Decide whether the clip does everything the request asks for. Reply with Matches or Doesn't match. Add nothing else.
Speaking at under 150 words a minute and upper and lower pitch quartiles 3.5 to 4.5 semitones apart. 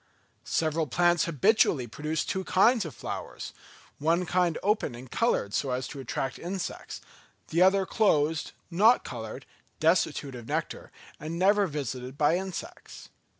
Doesn't match